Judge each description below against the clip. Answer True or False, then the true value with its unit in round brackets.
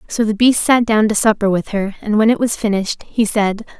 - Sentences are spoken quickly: True (255 wpm)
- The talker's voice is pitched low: False (215 Hz)